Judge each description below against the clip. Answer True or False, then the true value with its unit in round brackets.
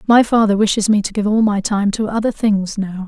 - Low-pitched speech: False (210 Hz)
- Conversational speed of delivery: False (255 wpm)